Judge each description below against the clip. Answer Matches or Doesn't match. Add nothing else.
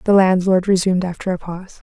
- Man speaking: Doesn't match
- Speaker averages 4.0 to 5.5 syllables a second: Doesn't match